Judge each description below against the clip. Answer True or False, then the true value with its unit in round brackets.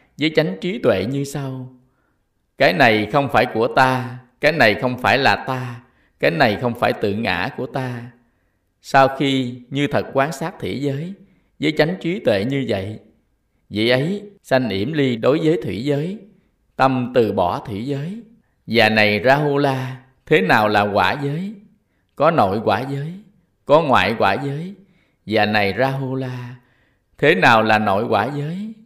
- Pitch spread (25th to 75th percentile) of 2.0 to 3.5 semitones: False (4.9 semitones)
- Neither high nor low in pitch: False (130 Hz)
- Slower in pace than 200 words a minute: True (175 wpm)